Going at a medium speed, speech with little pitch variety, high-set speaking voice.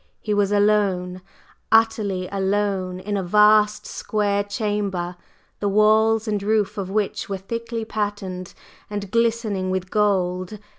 No: slow, 130 wpm; narrow, 1.9 semitones; high, 205 Hz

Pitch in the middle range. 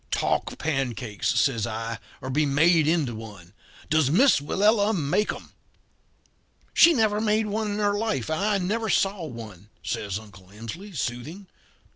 Yes: medium, 155 Hz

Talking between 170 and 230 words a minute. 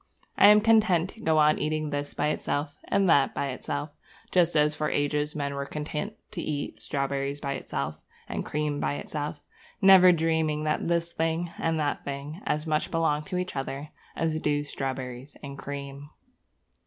Yes: average, 175 wpm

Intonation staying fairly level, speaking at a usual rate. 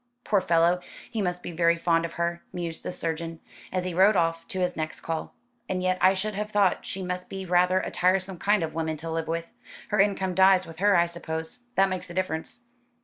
No: narrow, 2.3 semitones; fast, 225 wpm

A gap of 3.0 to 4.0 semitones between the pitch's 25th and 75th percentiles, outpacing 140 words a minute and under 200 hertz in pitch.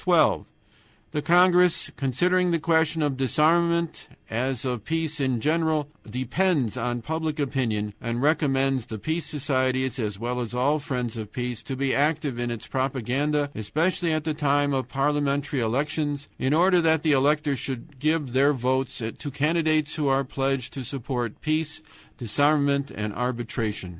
Yes: average, 3.7 semitones; average, 155 wpm; medium, 140 Hz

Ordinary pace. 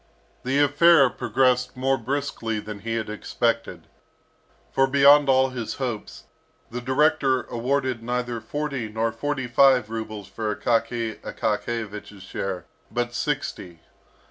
No: slow, 120 wpm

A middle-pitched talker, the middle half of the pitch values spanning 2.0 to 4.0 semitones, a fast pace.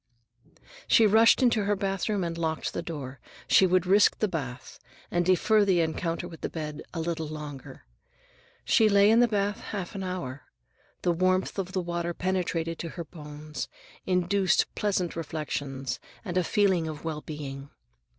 No: medium, 175 Hz; average, 3.7 semitones; average, 165 wpm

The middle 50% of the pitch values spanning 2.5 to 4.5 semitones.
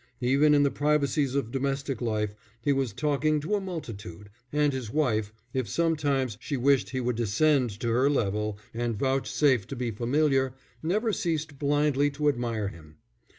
Yes: average, 4.2 semitones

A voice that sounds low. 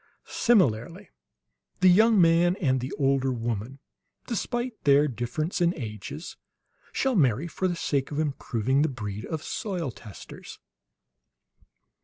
No: medium, 145 Hz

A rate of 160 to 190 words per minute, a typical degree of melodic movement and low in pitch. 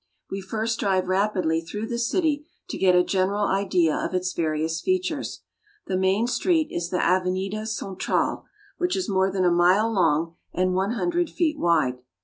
No: average, 180 wpm; average, 3.8 semitones; high, 190 Hz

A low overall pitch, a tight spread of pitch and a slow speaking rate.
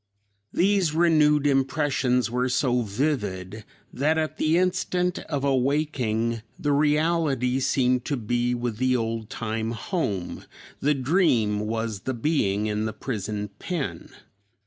No: low, 125 Hz; average, 5.1 semitones; slow, 125 wpm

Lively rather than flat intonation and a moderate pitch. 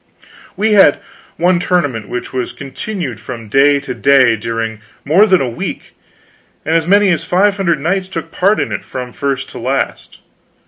Yes: wide, 6.7 semitones; medium, 145 Hz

